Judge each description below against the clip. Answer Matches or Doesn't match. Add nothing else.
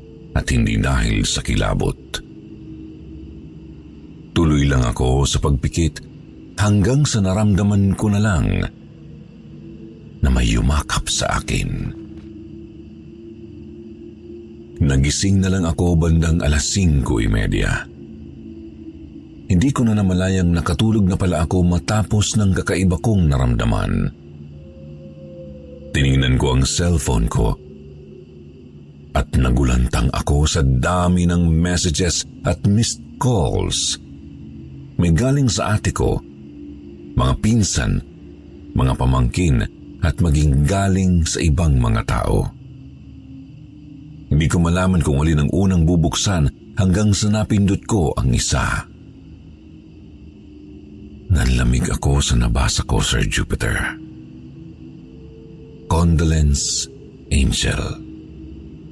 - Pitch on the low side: Matches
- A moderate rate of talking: Doesn't match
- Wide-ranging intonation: Matches